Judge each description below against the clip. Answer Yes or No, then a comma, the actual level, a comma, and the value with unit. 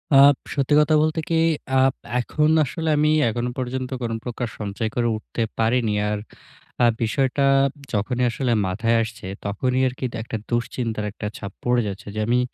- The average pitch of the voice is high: No, low, 120 Hz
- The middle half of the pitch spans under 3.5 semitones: Yes, average, 3.0 semitones